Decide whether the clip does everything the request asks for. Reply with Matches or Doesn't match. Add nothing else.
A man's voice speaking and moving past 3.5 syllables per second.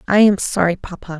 Doesn't match